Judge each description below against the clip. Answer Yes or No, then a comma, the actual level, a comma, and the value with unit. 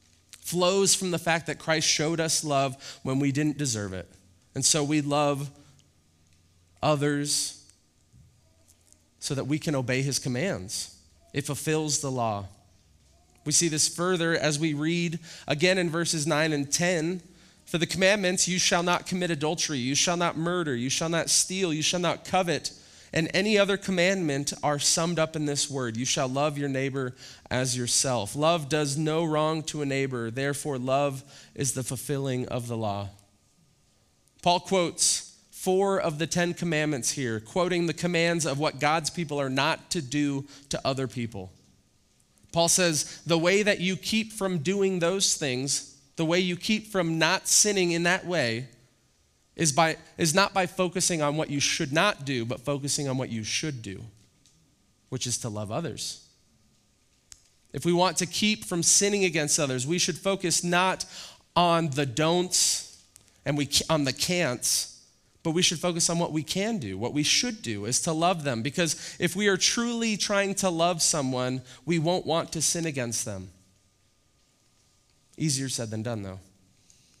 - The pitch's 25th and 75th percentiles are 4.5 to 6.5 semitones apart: Yes, average, 5.3 semitones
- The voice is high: No, medium, 150 Hz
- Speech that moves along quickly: No, average, 170 wpm